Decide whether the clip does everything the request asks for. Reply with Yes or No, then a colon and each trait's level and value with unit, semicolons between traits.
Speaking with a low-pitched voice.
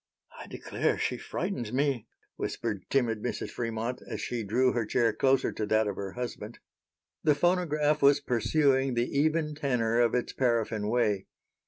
Yes: low, 125 Hz